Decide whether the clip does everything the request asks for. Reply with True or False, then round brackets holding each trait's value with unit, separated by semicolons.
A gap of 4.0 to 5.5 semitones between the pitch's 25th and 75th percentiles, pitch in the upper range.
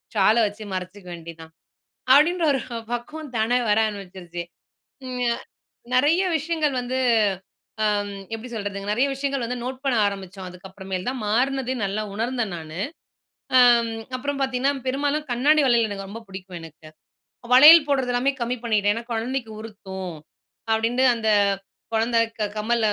True (4.7 semitones; 230 Hz)